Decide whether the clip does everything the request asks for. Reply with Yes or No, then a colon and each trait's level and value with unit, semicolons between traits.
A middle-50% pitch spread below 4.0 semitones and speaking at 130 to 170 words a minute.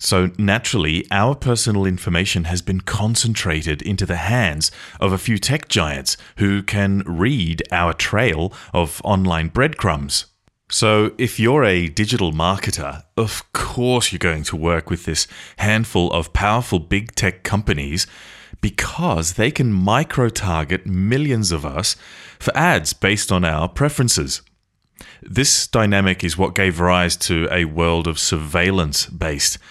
No: average, 4.3 semitones; average, 140 wpm